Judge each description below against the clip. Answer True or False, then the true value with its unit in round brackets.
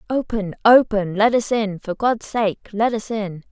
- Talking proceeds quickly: False (190 wpm)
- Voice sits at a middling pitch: False (215 Hz)